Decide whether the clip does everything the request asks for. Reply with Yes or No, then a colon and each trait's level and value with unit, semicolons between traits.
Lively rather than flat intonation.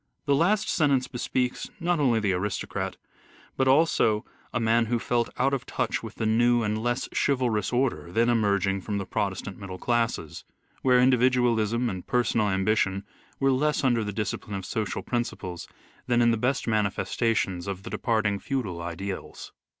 No: average, 3.7 semitones